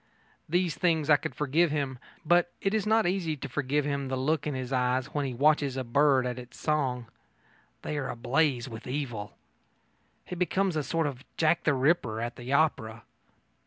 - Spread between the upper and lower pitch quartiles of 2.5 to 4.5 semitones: Yes, average, 3.7 semitones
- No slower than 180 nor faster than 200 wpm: Yes, average, 190 wpm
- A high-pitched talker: No, medium, 145 Hz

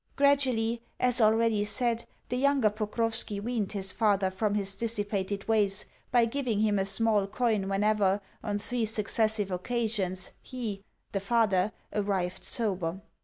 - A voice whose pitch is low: No, high, 215 Hz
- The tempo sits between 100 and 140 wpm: Yes, slow, 135 wpm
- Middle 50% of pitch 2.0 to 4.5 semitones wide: Yes, average, 2.7 semitones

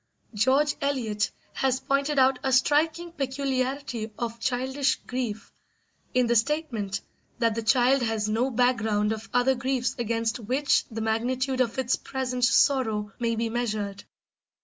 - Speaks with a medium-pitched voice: No, very high, 250 Hz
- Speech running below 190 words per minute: Yes, average, 140 wpm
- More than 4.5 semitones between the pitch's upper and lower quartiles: No, average, 3.0 semitones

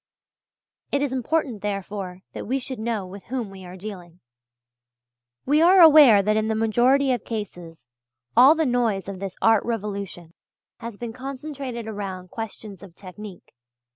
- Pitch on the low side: No, high, 220 Hz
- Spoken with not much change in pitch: No, average, 4.6 semitones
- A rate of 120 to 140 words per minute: No, average, 155 wpm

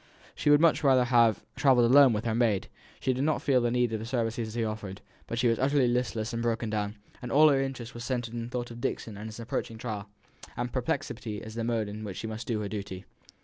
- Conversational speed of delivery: No, fast, 250 wpm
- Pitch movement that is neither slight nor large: No, narrow, 2.2 semitones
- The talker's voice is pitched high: No, low, 115 Hz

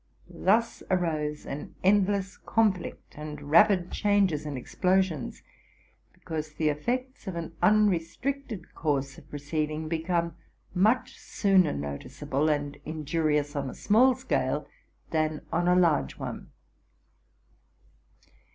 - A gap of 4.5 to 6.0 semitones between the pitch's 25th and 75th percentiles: Yes, average, 4.8 semitones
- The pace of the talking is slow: Yes, slow, 115 wpm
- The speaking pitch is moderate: Yes, medium, 165 Hz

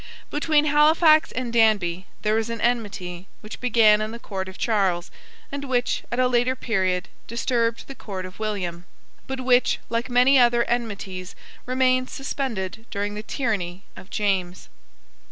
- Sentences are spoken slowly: No, average, 155 wpm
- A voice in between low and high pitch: No, high, 225 Hz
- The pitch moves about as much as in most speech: Yes, average, 4.6 semitones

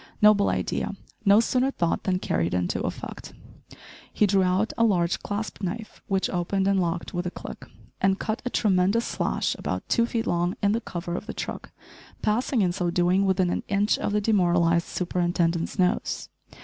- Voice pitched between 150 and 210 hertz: Yes, high, 190 Hz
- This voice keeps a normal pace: Yes, average, 180 wpm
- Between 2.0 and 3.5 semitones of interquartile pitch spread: Yes, average, 3.1 semitones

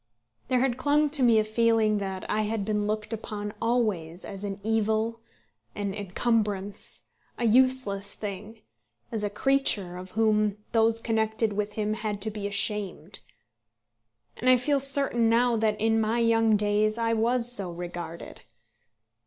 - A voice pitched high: Yes, high, 215 Hz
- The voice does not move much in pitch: Yes, narrow, 2.0 semitones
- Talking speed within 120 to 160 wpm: Yes, average, 155 wpm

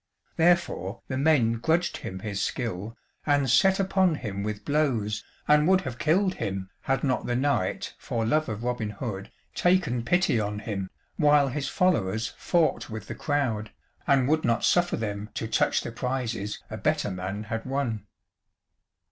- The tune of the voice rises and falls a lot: Yes, wide, 6.0 semitones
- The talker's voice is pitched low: Yes, low, 120 Hz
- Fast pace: No, average, 165 wpm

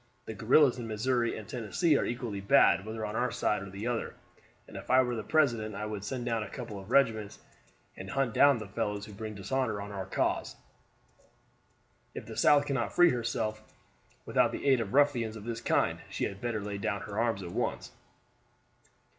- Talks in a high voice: No, low, 110 Hz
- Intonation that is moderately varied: Yes, average, 3.1 semitones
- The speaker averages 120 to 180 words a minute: No, average, 200 wpm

